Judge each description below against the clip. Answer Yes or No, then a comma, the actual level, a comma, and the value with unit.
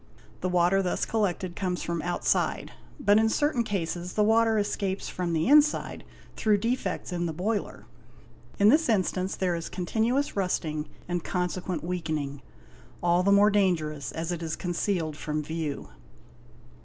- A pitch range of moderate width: Yes, average, 3.6 semitones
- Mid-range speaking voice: Yes, medium, 180 Hz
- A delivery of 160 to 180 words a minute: No, average, 150 wpm